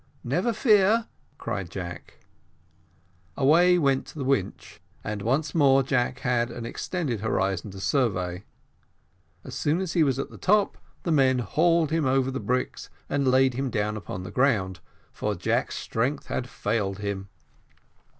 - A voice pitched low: Yes, low, 130 Hz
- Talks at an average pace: Yes, average, 150 wpm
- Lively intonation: Yes, wide, 6.2 semitones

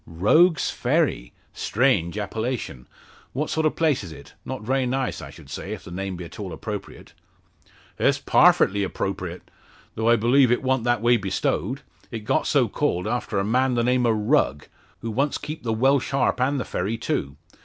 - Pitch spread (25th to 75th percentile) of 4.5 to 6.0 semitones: Yes, average, 5.1 semitones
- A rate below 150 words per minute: No, average, 185 wpm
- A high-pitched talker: No, low, 115 Hz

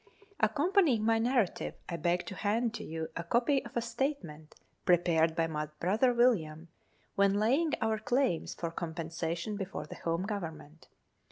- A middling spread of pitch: No, wide, 6.2 semitones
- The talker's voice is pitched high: Yes, high, 195 Hz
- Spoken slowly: No, average, 160 wpm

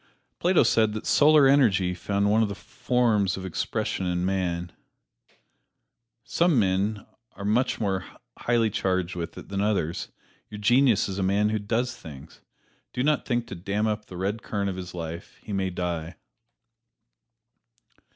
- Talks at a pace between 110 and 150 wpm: No, average, 160 wpm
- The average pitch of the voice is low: Yes, low, 100 Hz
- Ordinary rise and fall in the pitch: Yes, average, 3.5 semitones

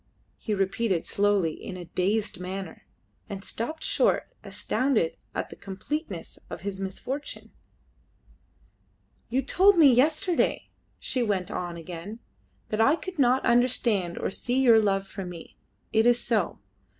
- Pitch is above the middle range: Yes, high, 215 Hz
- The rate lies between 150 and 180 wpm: No, average, 140 wpm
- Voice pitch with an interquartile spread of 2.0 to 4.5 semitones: No, average, 5.2 semitones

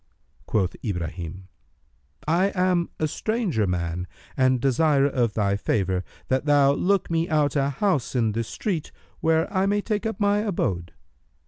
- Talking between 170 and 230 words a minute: No, average, 150 wpm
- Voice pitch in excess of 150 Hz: No, medium, 140 Hz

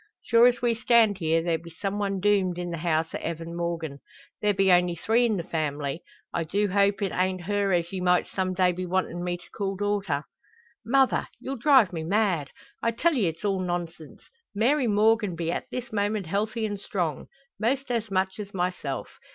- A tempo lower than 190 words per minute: No, average, 200 wpm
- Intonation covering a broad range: No, average, 3.8 semitones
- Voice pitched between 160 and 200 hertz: Yes, high, 190 Hz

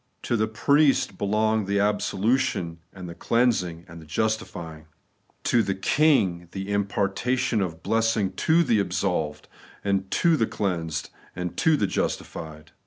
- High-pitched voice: No, low, 100 Hz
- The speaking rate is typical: No, slow, 130 wpm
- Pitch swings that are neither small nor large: Yes, average, 4.4 semitones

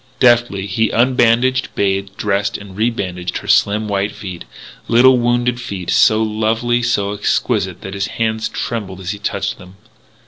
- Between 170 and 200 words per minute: No, average, 150 wpm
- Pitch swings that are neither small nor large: Yes, average, 3.3 semitones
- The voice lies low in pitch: Yes, low, 110 Hz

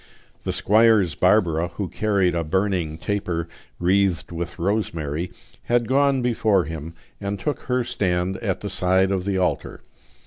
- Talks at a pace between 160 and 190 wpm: No, average, 145 wpm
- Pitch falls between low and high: No, very low, 95 Hz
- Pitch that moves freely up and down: No, average, 3.5 semitones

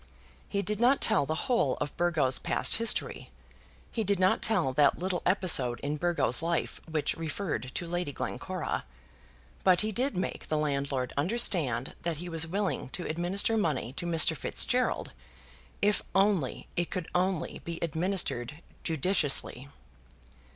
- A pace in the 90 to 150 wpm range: Yes, average, 145 wpm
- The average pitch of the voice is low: No, medium, 170 Hz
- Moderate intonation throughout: Yes, average, 4.7 semitones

